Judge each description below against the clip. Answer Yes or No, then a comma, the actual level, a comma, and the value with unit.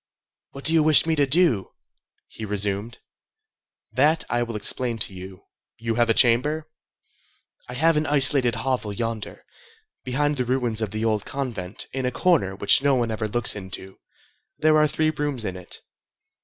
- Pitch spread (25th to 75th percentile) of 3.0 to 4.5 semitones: No, average, 5.3 semitones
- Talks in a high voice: No, low, 120 Hz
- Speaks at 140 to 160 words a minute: No, average, 170 wpm